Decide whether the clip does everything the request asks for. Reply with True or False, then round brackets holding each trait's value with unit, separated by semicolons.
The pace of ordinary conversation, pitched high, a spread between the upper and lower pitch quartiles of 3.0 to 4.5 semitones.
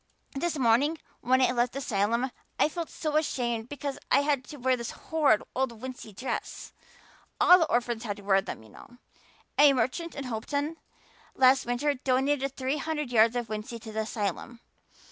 True (180 wpm; 255 Hz; 3.7 semitones)